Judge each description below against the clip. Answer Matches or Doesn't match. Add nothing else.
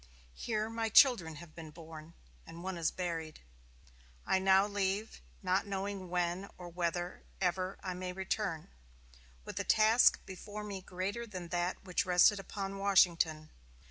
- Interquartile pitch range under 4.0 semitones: Matches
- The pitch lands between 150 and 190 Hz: Matches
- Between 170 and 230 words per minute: Doesn't match